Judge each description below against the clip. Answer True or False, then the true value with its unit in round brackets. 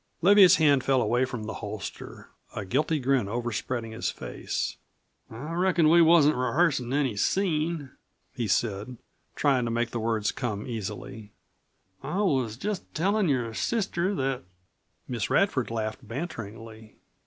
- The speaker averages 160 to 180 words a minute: False (140 wpm)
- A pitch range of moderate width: False (5.9 semitones)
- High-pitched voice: False (130 Hz)